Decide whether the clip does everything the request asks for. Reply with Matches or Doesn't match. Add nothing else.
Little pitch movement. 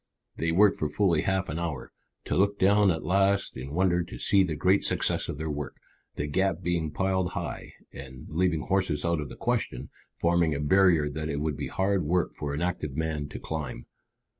Doesn't match